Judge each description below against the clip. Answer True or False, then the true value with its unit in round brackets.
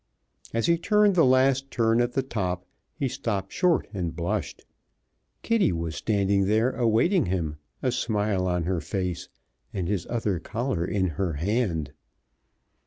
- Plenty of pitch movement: True (5.9 semitones)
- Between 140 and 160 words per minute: True (150 wpm)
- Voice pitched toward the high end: False (105 Hz)